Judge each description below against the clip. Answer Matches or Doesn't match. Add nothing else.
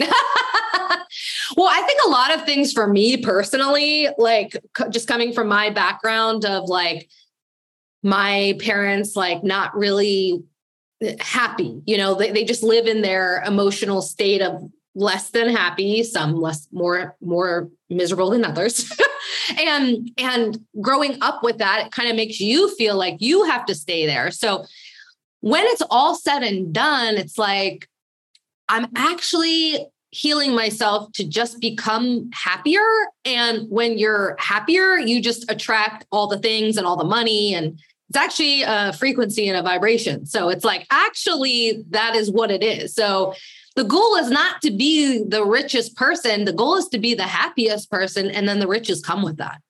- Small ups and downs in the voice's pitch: Doesn't match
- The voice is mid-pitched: Doesn't match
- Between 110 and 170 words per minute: Matches